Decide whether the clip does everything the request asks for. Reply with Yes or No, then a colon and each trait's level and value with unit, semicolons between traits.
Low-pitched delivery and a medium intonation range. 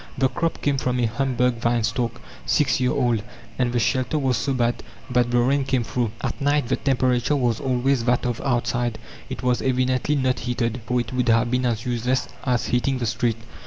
No: low, 125 Hz; narrow, 1.6 semitones